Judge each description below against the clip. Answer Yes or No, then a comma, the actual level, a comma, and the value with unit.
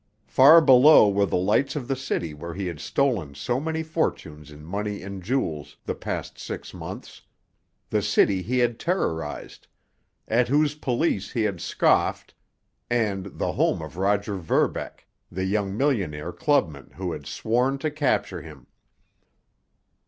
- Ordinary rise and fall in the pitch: No, wide, 6.9 semitones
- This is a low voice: Yes, low, 105 Hz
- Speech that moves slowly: No, average, 150 wpm